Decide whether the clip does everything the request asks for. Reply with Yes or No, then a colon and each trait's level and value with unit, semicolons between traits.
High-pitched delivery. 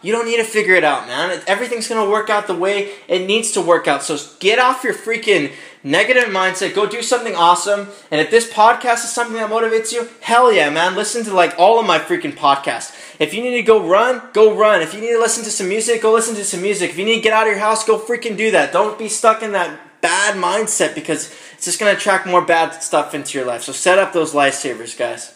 Yes: high, 215 Hz